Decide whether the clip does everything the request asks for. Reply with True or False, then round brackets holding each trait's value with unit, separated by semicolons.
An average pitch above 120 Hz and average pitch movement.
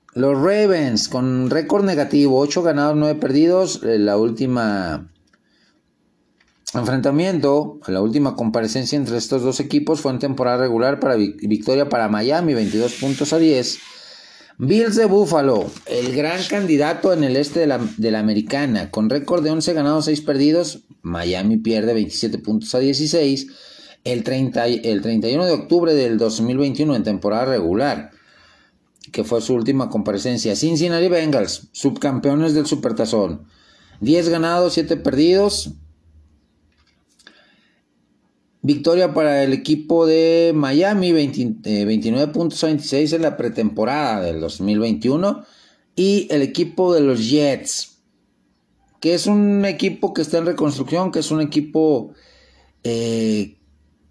False (140 Hz; 6.3 semitones)